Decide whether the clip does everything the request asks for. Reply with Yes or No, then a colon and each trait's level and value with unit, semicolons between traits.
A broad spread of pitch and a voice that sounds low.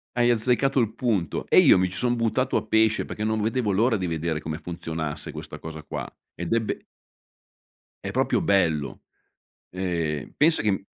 Yes: wide, 5.7 semitones; low, 100 Hz